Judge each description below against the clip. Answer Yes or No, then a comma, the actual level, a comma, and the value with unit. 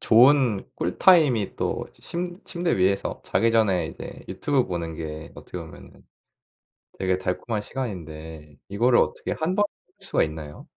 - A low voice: Yes, low, 100 Hz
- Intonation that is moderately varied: No, wide, 8.3 semitones